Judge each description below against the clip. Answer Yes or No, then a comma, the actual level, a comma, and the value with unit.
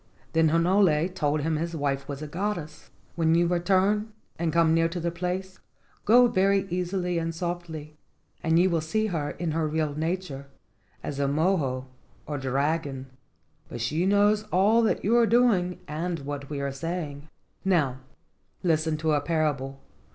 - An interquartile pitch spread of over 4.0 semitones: No, average, 3.6 semitones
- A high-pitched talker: No, medium, 165 Hz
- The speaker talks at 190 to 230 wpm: No, average, 165 wpm